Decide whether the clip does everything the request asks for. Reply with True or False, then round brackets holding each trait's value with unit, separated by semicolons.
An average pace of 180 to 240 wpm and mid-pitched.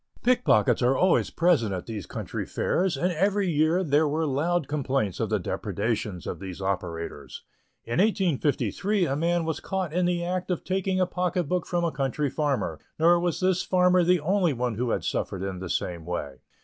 True (190 wpm; 160 Hz)